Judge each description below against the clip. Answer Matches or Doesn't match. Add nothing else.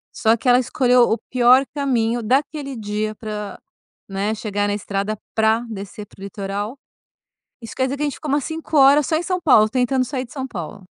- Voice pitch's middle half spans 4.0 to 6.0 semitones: Matches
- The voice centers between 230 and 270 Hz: Matches